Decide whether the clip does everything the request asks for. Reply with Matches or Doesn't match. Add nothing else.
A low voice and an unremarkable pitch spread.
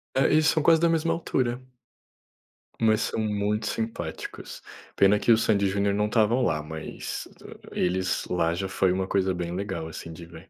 Matches